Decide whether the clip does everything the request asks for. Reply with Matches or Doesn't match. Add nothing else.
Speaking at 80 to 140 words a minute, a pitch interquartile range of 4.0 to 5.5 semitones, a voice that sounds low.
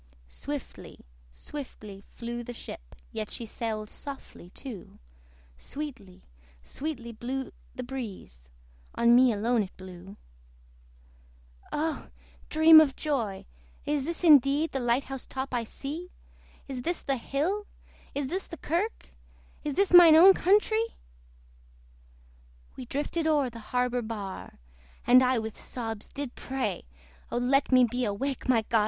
Doesn't match